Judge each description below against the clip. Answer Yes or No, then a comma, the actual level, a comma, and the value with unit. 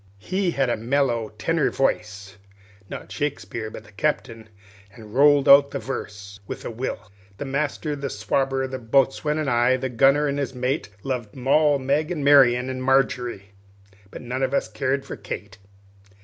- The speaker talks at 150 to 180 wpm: Yes, average, 170 wpm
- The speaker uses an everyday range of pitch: Yes, average, 3.5 semitones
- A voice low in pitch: Yes, low, 130 Hz